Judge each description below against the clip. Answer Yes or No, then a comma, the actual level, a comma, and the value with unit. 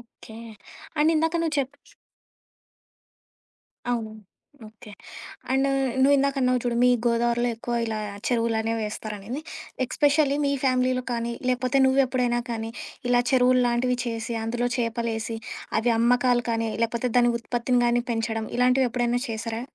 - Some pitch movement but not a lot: No, narrow, 1.8 semitones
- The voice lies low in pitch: No, high, 240 Hz